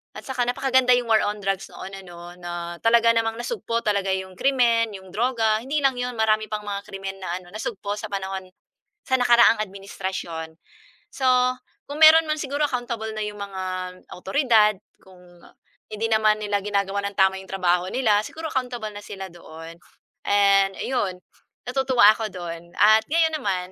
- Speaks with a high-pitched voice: Yes, high, 210 Hz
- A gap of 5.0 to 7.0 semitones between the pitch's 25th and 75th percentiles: No, average, 4.0 semitones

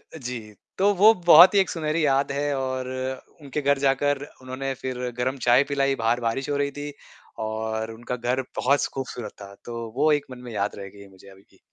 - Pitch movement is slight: No, average, 3.5 semitones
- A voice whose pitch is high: No, low, 130 Hz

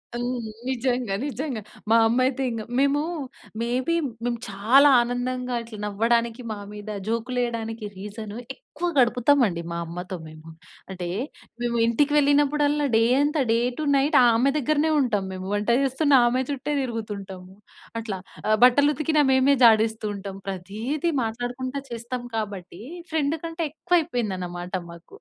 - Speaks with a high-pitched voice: Yes, high, 240 Hz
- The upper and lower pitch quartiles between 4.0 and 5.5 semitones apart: Yes, average, 4.7 semitones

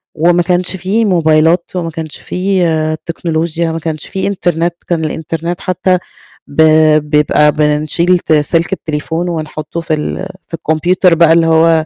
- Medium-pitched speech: Yes, medium, 165 Hz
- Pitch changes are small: Yes, narrow, 2.1 semitones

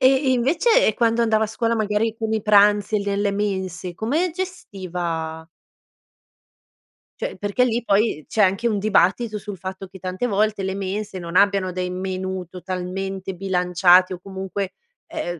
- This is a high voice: Yes, high, 195 Hz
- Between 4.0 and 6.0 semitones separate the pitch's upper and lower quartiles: No, average, 2.9 semitones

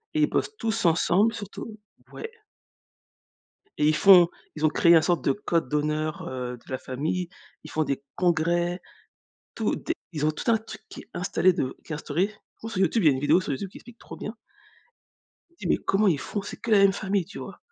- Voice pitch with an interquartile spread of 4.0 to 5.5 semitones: Yes, average, 4.8 semitones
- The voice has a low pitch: No, medium, 175 Hz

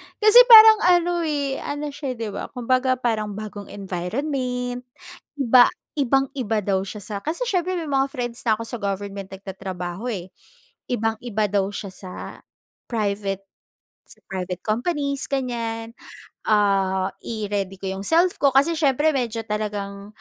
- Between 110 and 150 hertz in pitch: No, high, 225 Hz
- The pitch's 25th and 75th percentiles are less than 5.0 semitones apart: No, wide, 5.5 semitones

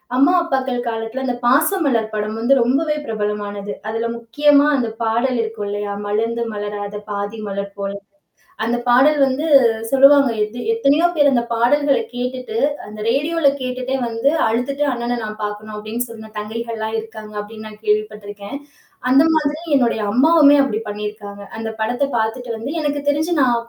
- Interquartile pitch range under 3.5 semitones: No, average, 4.3 semitones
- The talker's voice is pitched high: Yes, high, 235 Hz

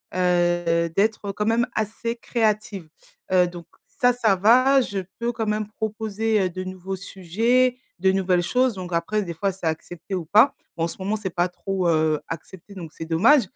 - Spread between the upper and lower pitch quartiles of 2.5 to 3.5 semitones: No, average, 3.9 semitones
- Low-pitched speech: No, high, 195 Hz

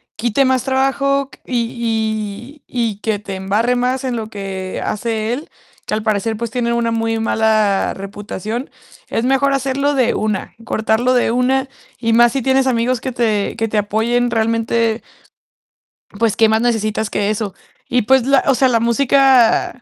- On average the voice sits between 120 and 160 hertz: No, high, 230 Hz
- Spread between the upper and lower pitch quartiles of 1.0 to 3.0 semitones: Yes, average, 2.7 semitones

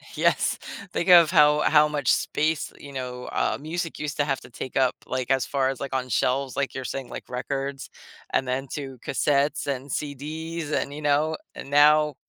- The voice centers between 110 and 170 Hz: Yes, medium, 140 Hz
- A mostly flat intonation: Yes, narrow, 2.3 semitones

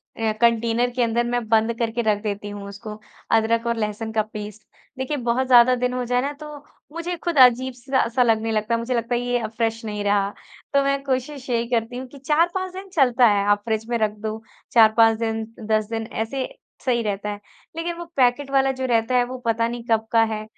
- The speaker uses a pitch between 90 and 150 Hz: No, high, 235 Hz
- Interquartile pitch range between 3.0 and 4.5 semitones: No, narrow, 2.6 semitones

